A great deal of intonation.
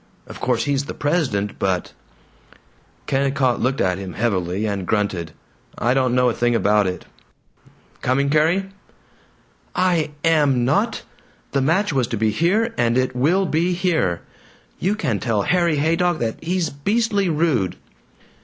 Yes: wide, 7.3 semitones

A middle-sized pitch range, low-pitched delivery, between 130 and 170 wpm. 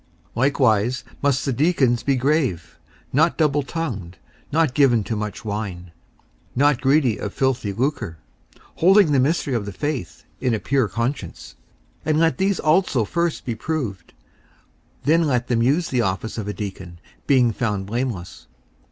No: wide, 5.8 semitones; low, 125 Hz; average, 160 wpm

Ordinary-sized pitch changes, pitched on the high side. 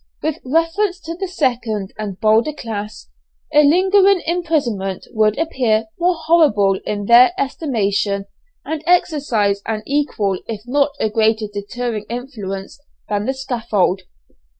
No: wide, 6.8 semitones; high, 240 Hz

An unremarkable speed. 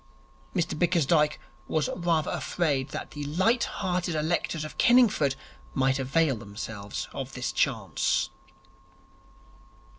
No: slow, 110 wpm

